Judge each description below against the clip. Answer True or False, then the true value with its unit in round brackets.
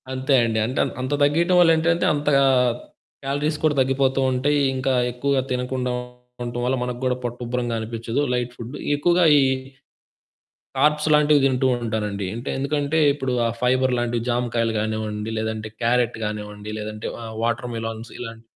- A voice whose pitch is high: False (125 Hz)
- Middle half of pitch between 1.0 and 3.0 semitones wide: False (3.4 semitones)